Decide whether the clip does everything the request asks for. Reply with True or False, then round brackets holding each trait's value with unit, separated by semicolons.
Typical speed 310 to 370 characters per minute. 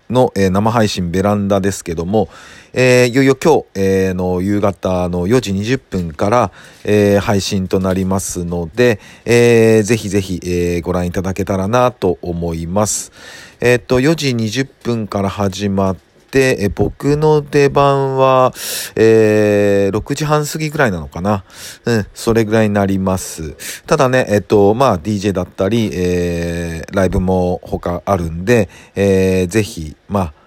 False (280 characters per minute)